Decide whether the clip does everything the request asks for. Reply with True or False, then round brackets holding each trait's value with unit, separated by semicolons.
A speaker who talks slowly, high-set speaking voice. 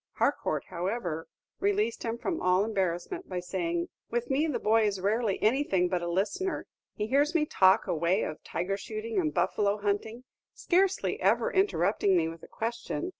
False (170 wpm; 210 Hz)